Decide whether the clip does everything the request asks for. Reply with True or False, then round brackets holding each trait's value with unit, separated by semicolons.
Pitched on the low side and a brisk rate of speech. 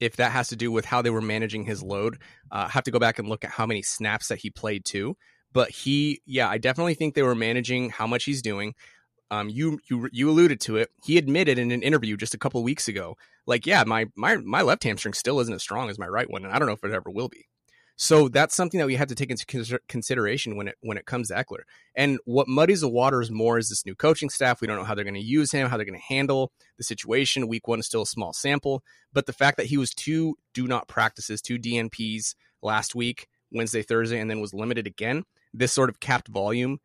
True (120 Hz; 260 wpm)